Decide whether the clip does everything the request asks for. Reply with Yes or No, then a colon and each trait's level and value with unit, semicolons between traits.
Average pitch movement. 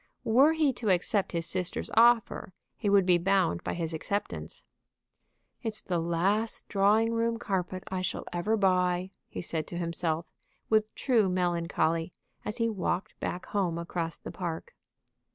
Yes: average, 4.0 semitones